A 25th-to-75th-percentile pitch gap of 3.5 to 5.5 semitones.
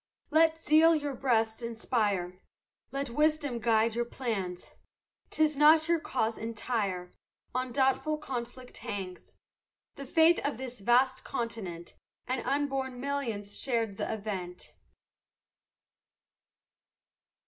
Yes: average, 4.4 semitones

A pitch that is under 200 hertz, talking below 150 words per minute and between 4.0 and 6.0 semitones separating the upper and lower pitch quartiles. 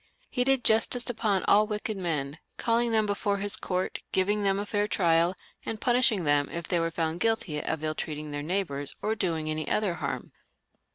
No: high, 190 Hz; average, 195 wpm; average, 5.0 semitones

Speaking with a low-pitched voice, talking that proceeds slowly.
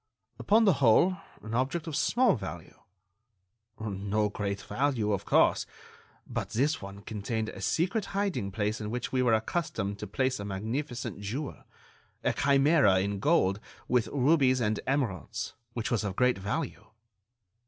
No: low, 115 Hz; average, 155 wpm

